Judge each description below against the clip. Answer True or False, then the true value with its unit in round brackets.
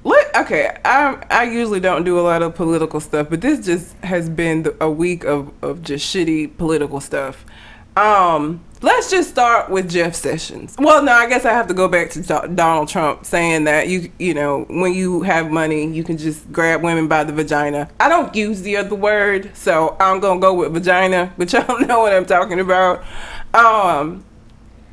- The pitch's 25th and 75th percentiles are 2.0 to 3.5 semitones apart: False (4.0 semitones)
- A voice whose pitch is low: False (175 Hz)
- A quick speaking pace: False (195 wpm)